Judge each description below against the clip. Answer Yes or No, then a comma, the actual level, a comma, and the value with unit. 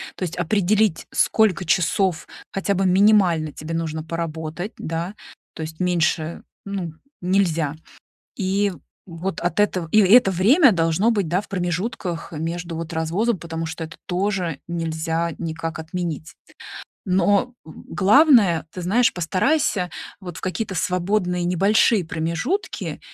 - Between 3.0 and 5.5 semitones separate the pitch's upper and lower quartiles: Yes, average, 3.3 semitones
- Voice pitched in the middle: Yes, medium, 180 Hz